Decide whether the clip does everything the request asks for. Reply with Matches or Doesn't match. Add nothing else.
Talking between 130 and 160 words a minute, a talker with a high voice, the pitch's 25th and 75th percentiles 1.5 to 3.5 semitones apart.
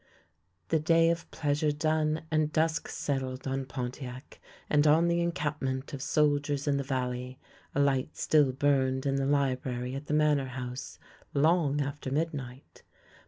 Doesn't match